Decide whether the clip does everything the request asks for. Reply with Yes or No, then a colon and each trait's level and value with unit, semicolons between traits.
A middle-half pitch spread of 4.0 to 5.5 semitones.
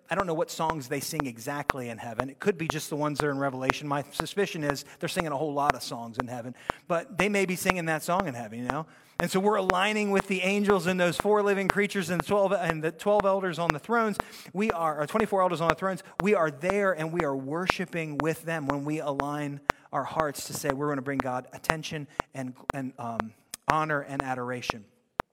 Yes: average, 4.9 semitones